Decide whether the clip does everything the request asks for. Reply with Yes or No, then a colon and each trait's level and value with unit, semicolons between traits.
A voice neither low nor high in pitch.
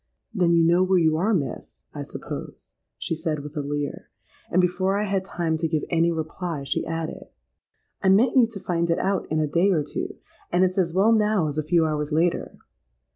Yes: medium, 170 Hz